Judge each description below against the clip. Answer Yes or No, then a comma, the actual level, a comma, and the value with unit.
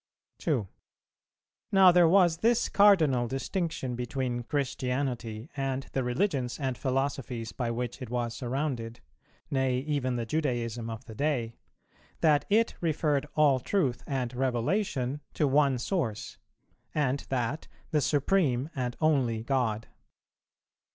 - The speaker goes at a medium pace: No, slow, 125 wpm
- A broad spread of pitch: No, average, 3.8 semitones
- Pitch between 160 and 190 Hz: No, low, 130 Hz